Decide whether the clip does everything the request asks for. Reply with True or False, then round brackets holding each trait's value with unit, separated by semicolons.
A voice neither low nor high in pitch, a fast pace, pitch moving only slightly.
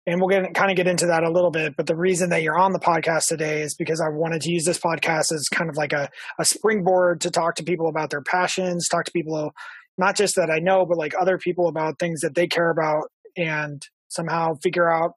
True (170 Hz; 255 wpm; 1.9 semitones)